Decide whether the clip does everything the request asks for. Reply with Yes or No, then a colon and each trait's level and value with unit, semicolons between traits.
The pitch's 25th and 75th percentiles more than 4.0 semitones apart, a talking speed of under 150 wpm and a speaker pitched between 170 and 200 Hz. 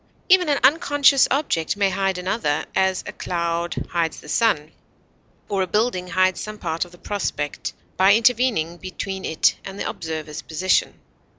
No: average, 4.4 semitones; average, 160 wpm; medium, 185 Hz